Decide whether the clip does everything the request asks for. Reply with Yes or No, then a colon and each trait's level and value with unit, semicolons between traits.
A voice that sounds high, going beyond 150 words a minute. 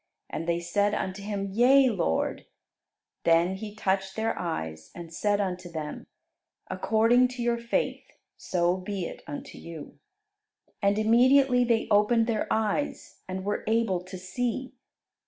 No: high, 205 Hz; average, 140 wpm